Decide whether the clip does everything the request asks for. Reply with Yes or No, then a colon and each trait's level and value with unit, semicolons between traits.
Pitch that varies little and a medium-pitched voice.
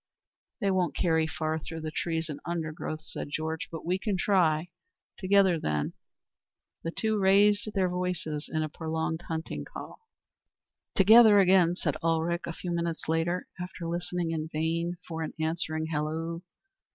Yes: narrow, 2.2 semitones; medium, 165 Hz